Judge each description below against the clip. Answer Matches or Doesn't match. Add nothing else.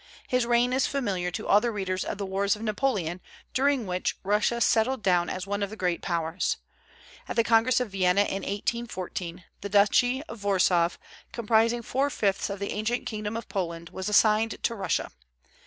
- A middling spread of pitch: Matches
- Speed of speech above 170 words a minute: Matches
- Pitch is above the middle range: Matches